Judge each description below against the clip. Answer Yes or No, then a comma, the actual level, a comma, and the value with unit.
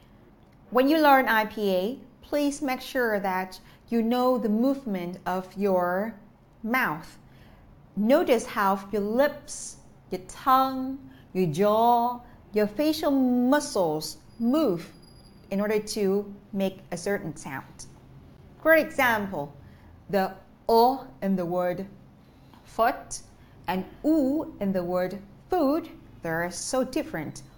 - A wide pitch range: Yes, wide, 5.8 semitones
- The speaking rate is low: Yes, slow, 110 wpm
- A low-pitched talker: No, high, 210 Hz